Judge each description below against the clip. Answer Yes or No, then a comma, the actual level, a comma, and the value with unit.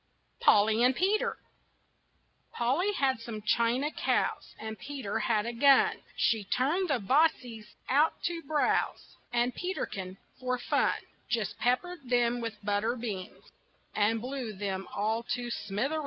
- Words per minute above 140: No, slow, 135 wpm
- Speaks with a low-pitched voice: No, high, 240 Hz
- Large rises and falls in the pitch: No, average, 4.5 semitones